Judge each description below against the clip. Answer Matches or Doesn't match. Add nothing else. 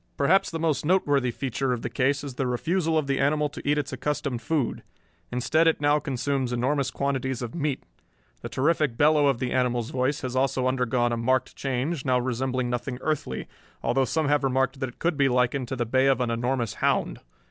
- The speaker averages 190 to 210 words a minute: Matches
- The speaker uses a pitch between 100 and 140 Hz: Matches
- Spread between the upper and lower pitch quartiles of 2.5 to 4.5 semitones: Matches